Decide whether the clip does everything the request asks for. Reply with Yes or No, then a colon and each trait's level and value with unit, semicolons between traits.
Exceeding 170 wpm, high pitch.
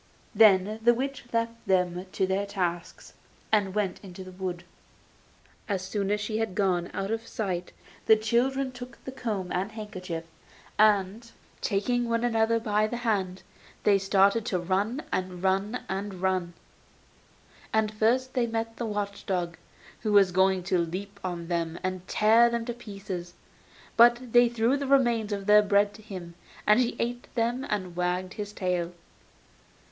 No: average, 165 wpm; high, 205 Hz